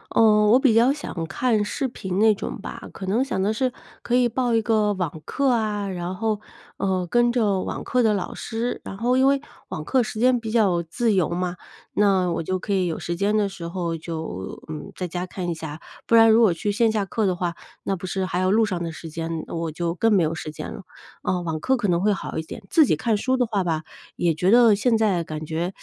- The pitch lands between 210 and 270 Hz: No, high, 195 Hz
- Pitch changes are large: No, average, 4.6 semitones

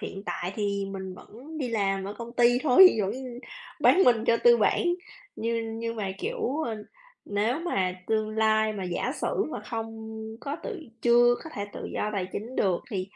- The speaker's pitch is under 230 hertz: Yes, high, 220 Hz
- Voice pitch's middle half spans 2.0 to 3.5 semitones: Yes, average, 3.2 semitones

